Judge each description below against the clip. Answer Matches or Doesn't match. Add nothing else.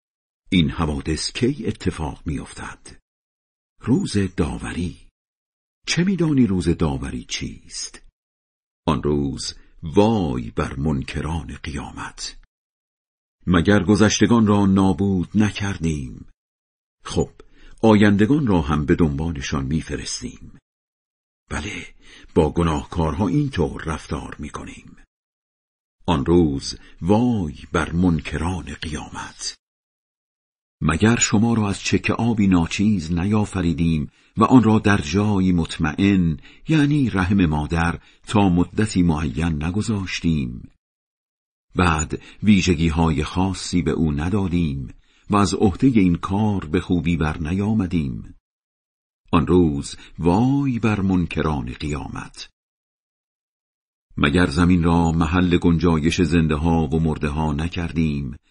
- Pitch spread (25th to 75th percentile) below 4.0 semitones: Doesn't match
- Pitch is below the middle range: Matches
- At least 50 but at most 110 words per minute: Matches